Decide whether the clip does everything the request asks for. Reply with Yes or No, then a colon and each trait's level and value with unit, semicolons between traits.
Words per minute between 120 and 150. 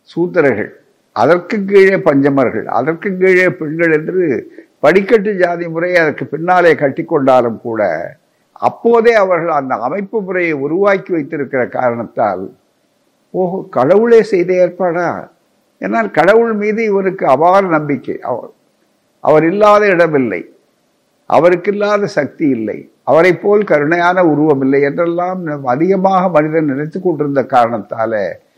No: average, 110 wpm